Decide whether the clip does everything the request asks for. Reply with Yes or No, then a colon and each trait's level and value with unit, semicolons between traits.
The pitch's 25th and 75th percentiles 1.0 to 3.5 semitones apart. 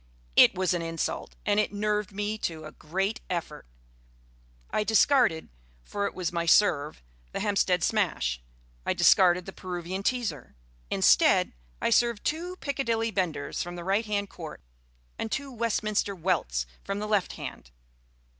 No: average, 3.9 semitones